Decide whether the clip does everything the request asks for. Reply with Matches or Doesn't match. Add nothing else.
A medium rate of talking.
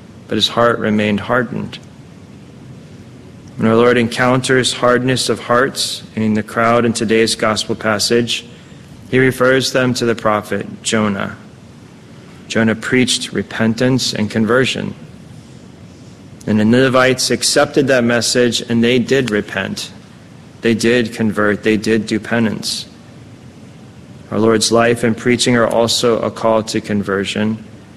Doesn't match